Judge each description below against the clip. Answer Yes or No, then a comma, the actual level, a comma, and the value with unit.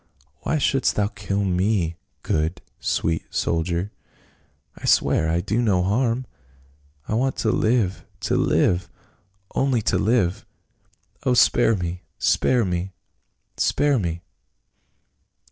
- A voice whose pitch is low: Yes, very low, 95 Hz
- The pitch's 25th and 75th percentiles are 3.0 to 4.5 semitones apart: No, average, 5.0 semitones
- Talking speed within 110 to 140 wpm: Yes, slow, 135 wpm